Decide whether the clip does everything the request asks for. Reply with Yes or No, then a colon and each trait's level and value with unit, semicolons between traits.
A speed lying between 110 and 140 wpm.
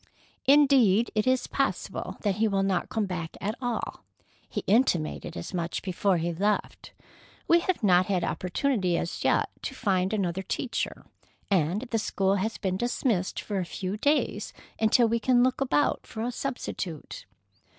No: average, 160 wpm